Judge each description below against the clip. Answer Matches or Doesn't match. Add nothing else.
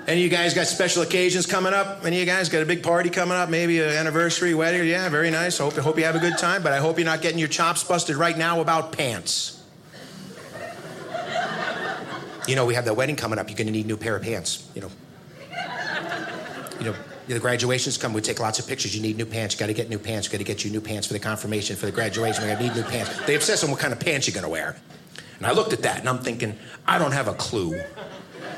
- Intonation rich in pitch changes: Matches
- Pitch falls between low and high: Matches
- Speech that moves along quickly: Matches